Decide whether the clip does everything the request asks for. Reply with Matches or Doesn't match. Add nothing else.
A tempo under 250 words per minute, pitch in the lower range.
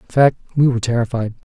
Matches